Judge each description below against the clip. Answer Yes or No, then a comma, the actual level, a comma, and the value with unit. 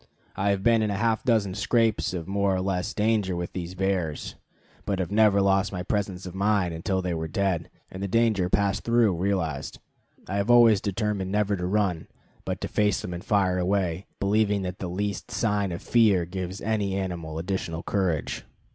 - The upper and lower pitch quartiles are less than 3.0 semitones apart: Yes, narrow, 2.4 semitones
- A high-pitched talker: No, very low, 95 Hz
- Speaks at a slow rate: No, average, 190 wpm